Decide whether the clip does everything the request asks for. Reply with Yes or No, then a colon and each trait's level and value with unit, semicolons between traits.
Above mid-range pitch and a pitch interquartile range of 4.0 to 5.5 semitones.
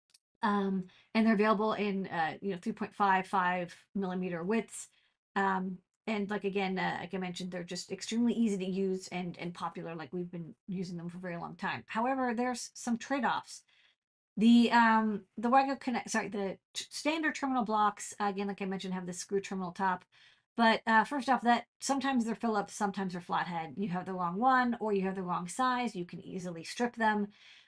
No: high, 200 Hz; average, 3.6 semitones